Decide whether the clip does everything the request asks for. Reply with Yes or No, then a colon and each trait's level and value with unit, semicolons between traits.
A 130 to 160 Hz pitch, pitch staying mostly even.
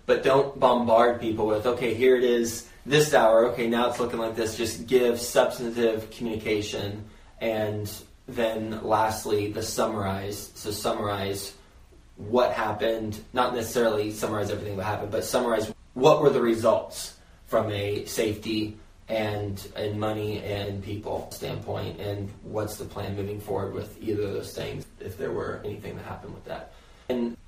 No: low, 110 Hz; narrow, 2.2 semitones